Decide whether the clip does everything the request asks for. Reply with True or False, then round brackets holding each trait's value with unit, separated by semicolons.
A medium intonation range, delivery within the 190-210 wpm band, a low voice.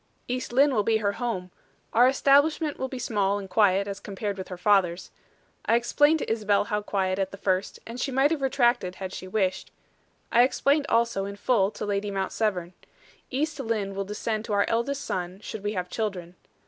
False (4.2 semitones; 200 wpm; 210 Hz)